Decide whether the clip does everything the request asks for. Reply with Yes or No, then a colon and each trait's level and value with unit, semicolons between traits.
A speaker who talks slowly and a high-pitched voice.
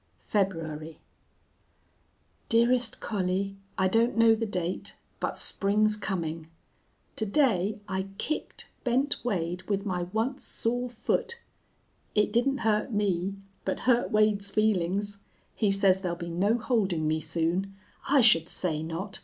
Yes: slow, 130 wpm; high, 200 Hz